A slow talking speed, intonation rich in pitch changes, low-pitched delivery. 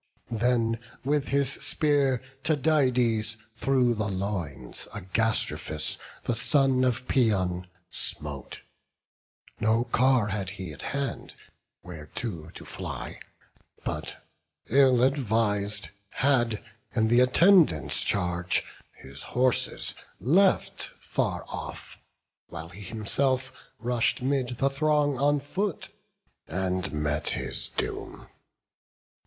Yes: slow, 100 wpm; wide, 5.8 semitones; low, 120 Hz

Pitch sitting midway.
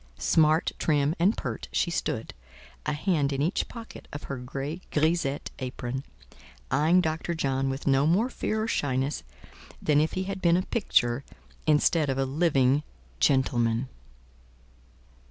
Yes: medium, 150 Hz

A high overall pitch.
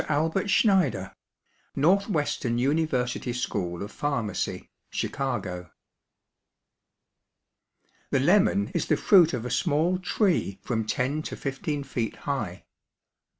No: medium, 140 Hz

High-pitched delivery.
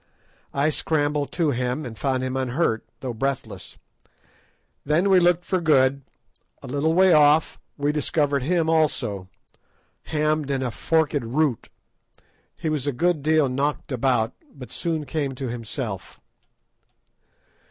No: medium, 145 Hz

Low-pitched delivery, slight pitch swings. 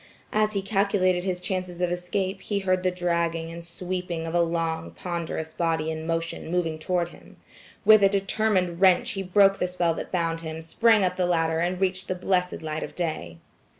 No: medium, 180 Hz; narrow, 2.1 semitones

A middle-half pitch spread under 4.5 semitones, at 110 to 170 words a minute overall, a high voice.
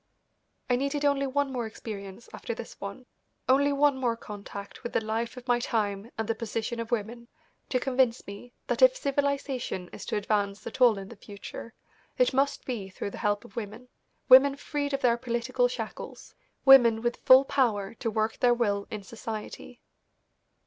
No: average, 3.4 semitones; average, 180 wpm; high, 235 Hz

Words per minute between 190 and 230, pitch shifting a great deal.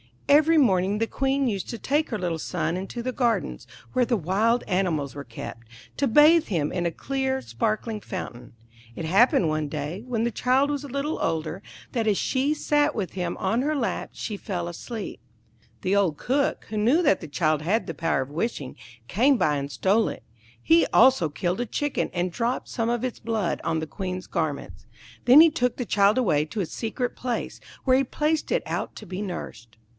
Yes: average, 200 wpm; wide, 7.0 semitones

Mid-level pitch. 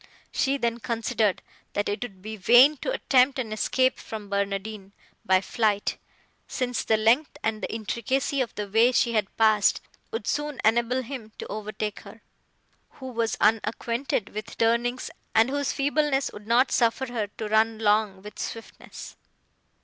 No: high, 225 Hz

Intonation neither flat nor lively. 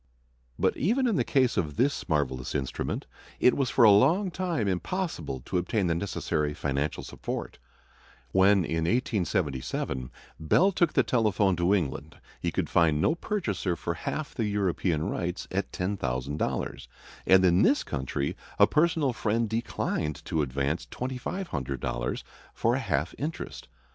No: wide, 9.0 semitones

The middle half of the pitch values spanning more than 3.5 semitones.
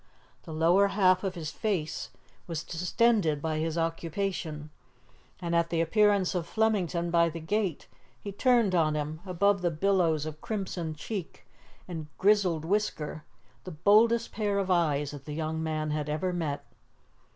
Yes: average, 4.1 semitones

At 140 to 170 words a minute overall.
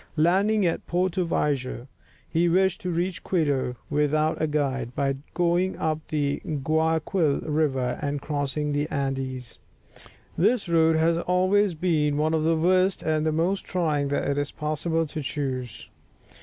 Yes: average, 145 wpm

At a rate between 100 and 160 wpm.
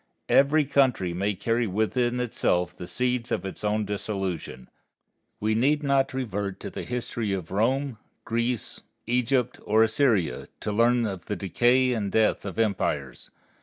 Yes: average, 150 wpm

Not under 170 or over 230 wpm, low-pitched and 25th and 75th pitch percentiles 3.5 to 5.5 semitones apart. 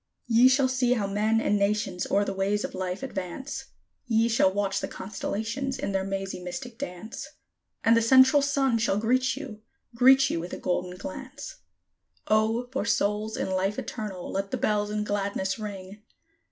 No: average, 175 wpm; high, 215 Hz; average, 4.3 semitones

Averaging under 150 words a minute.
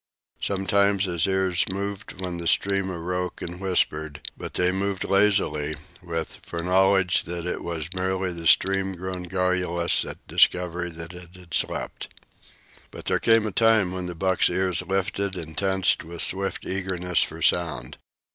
No: average, 155 wpm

